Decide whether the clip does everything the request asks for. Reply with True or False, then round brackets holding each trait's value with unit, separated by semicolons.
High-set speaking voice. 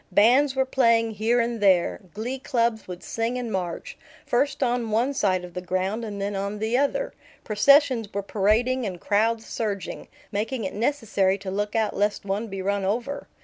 True (220 Hz)